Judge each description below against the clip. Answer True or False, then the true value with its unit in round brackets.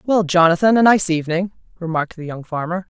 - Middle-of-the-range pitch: True (175 Hz)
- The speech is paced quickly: False (185 wpm)